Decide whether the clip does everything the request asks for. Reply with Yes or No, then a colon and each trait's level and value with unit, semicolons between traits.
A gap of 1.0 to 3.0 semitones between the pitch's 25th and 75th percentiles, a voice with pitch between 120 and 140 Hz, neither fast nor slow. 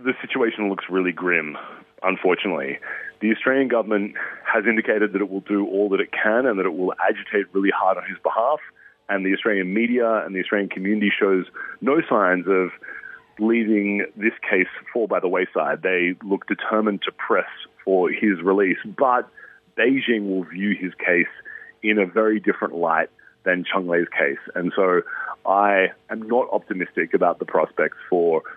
No: narrow, 2.6 semitones; low, 100 Hz; average, 170 wpm